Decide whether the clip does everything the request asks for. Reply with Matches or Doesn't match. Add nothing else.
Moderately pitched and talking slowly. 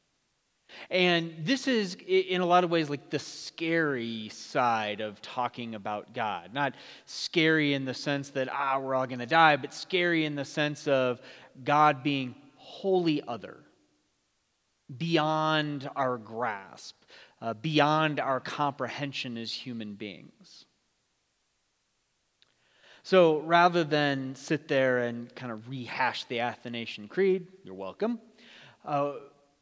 Matches